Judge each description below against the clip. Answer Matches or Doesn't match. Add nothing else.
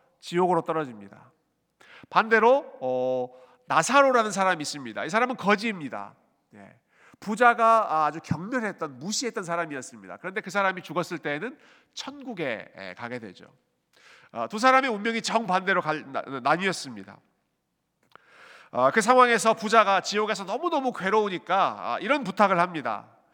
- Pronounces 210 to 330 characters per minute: Matches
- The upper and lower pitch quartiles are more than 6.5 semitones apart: Doesn't match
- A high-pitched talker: Matches